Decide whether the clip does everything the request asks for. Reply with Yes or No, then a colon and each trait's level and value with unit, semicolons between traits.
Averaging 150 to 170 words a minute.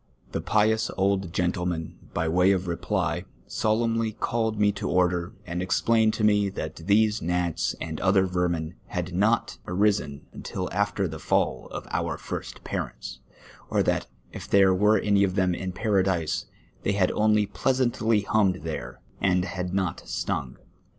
Yes: average, 155 wpm